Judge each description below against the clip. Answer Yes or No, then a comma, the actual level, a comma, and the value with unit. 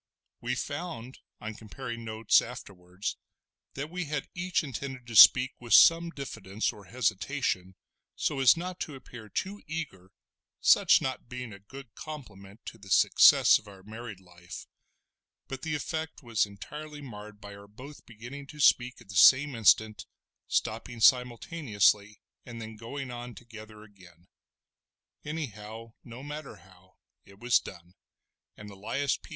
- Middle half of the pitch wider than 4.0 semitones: Yes, average, 5.0 semitones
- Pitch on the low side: Yes, low, 115 Hz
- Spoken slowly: No, average, 145 wpm